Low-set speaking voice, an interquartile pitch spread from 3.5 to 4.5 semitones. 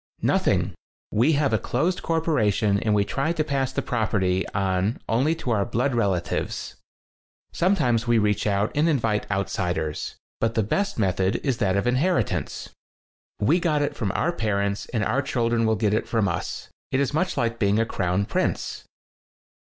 No: low, 115 Hz; wide, 5.6 semitones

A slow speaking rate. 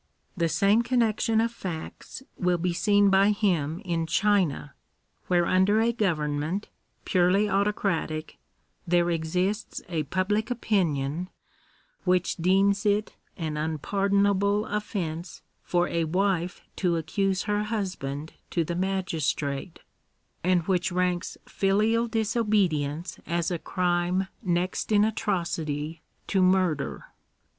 Yes: slow, 115 wpm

